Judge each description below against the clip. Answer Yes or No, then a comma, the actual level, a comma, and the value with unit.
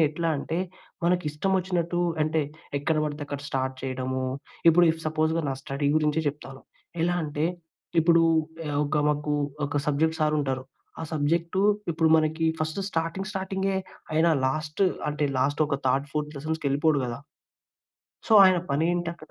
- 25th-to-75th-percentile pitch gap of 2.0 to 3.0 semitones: Yes, narrow, 2.6 semitones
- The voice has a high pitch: No, medium, 155 Hz